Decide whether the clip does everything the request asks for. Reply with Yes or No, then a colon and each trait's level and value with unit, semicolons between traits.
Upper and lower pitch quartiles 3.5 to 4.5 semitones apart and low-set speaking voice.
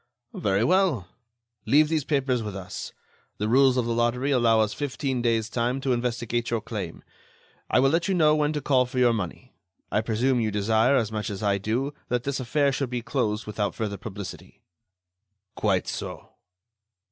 Yes: average, 3.8 semitones; low, 120 Hz